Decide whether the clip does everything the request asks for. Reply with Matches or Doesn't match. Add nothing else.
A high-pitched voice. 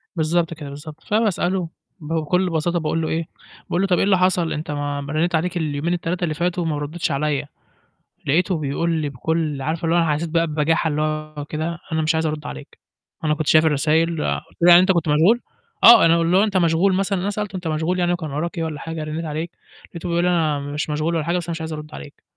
Doesn't match